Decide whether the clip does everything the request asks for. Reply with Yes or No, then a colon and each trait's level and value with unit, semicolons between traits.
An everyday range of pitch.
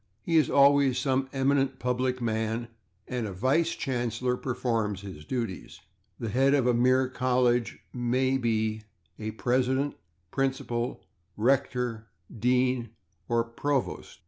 No: narrow, 2.3 semitones